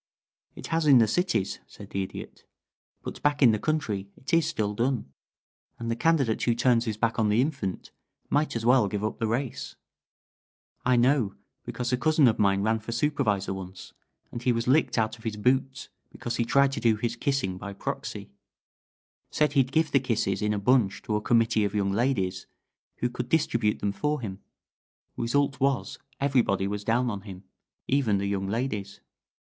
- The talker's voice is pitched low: Yes, low, 115 Hz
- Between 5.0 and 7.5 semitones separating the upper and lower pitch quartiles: No, average, 4.4 semitones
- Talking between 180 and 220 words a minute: Yes, average, 190 wpm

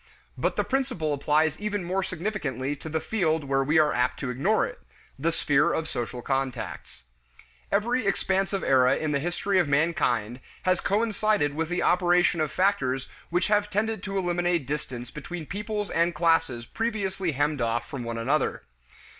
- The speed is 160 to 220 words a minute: Yes, average, 165 wpm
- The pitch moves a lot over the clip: Yes, wide, 6.0 semitones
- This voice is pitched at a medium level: Yes, medium, 165 Hz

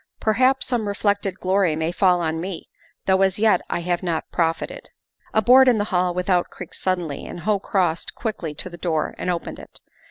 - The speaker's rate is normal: Yes, average, 195 wpm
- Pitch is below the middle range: No, medium, 185 Hz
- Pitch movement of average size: Yes, average, 3.1 semitones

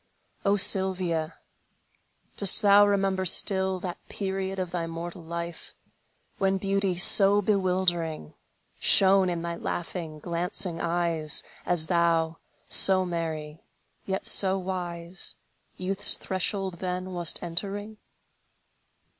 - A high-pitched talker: No, medium, 180 Hz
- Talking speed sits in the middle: No, slow, 105 wpm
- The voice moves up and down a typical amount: No, narrow, 2.2 semitones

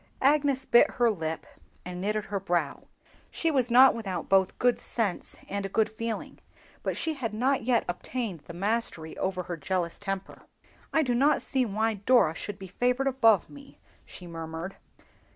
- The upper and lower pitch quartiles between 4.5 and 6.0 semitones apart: Yes, average, 5.2 semitones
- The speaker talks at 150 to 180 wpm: Yes, average, 170 wpm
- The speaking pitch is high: Yes, high, 215 Hz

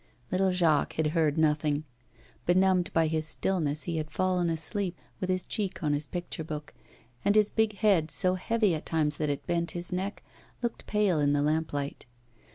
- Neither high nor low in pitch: Yes, medium, 170 Hz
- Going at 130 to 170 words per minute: No, average, 180 wpm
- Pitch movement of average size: Yes, average, 3.3 semitones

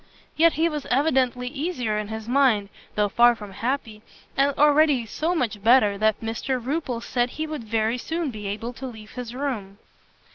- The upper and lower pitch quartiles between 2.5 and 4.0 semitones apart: No, average, 4.5 semitones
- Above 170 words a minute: Yes, average, 180 wpm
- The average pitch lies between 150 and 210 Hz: No, high, 245 Hz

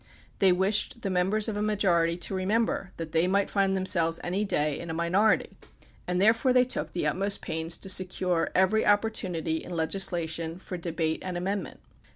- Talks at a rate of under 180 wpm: No, average, 185 wpm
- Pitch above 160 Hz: Yes, medium, 185 Hz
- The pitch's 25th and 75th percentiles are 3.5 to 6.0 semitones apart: No, average, 3.1 semitones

